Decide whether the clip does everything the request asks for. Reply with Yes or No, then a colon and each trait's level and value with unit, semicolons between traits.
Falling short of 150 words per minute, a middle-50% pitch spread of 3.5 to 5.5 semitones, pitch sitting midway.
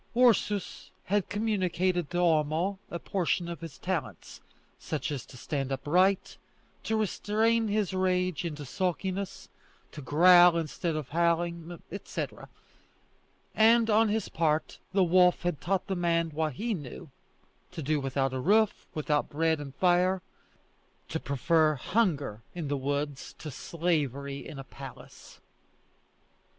Yes: slow, 135 wpm; average, 4.3 semitones; medium, 170 Hz